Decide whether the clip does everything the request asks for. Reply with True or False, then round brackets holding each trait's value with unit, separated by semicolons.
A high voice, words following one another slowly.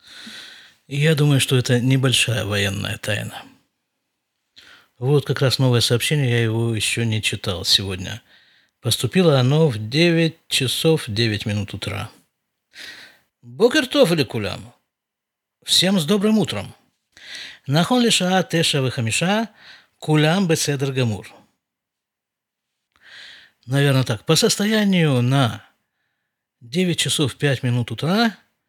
False (135 Hz; 105 wpm)